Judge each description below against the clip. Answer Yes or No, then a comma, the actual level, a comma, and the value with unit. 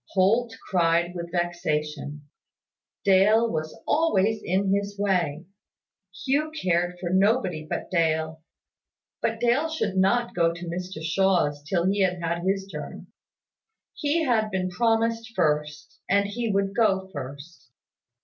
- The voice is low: No, medium, 185 Hz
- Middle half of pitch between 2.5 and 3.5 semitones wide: No, average, 4.5 semitones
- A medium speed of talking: No, slow, 130 wpm